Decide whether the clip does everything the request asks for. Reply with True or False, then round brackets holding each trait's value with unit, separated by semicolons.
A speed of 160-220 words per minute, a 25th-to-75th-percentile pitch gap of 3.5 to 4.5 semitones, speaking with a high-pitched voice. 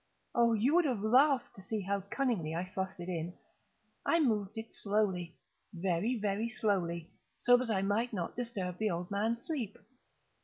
True (165 wpm; 4.2 semitones; 205 Hz)